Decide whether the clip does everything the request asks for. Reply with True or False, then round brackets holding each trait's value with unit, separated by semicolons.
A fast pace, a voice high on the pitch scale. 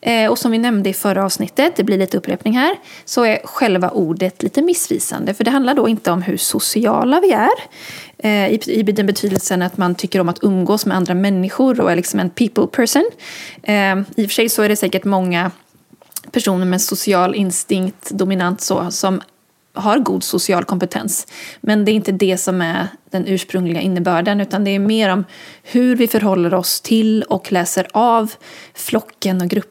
False (185 wpm; 195 Hz)